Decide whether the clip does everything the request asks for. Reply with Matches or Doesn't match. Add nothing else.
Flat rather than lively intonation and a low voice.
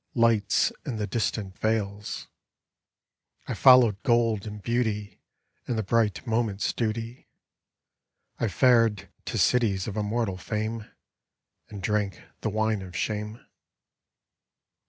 Matches